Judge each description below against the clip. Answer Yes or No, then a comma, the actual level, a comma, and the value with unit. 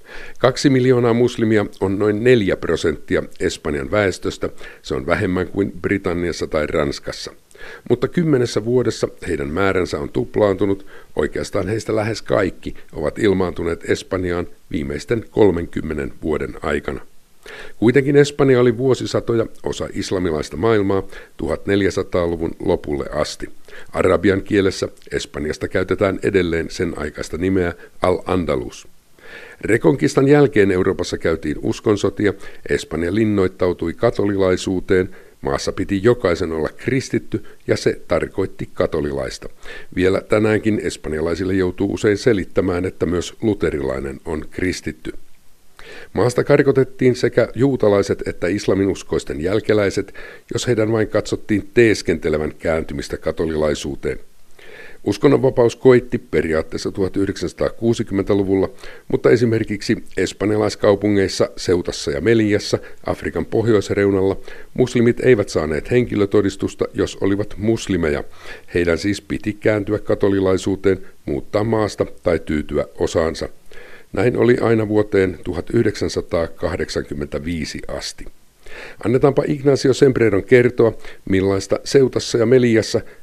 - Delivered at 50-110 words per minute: Yes, average, 100 wpm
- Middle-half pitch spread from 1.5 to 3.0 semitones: No, average, 3.8 semitones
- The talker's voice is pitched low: Yes, low, 105 Hz